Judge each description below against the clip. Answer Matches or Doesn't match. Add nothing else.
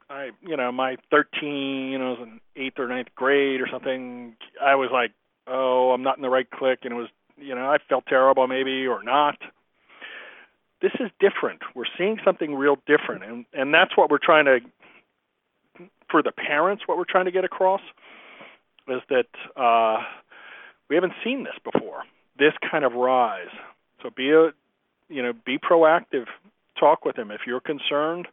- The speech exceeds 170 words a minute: Matches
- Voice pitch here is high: Doesn't match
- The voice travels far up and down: Doesn't match